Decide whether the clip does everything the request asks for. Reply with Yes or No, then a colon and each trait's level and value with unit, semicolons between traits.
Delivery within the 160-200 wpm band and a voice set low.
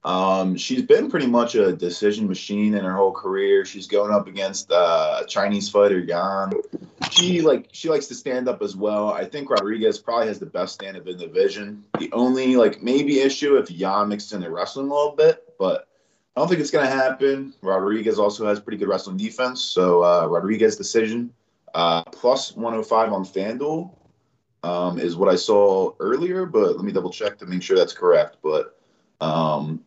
Yes: average, 195 wpm; low, 115 Hz